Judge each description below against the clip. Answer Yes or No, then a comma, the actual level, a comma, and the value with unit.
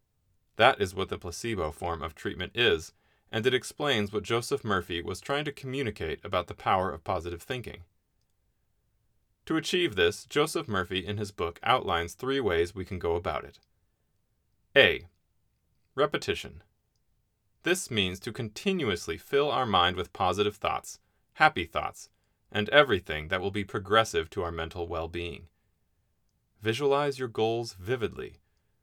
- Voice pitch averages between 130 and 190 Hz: No, low, 105 Hz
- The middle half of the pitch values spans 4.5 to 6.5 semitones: Yes, average, 5.0 semitones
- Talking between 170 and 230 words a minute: No, average, 145 wpm